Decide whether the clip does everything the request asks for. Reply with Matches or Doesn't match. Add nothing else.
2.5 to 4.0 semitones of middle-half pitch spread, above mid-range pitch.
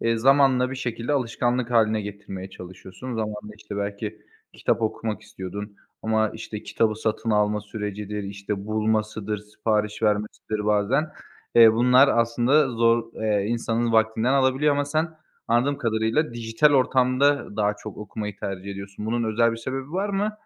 Doesn't match